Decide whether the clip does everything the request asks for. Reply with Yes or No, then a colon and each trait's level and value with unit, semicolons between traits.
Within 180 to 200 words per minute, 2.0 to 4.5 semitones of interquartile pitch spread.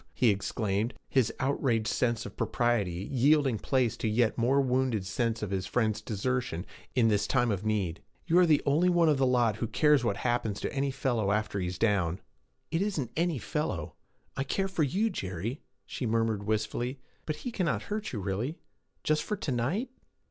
No: average, 190 wpm; average, 4.9 semitones